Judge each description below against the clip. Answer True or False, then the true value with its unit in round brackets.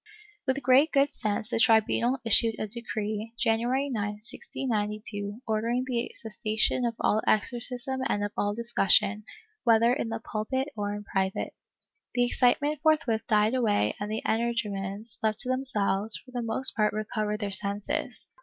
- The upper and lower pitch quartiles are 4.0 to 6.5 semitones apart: False (2.8 semitones)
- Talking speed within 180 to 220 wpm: False (155 wpm)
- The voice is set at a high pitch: True (225 Hz)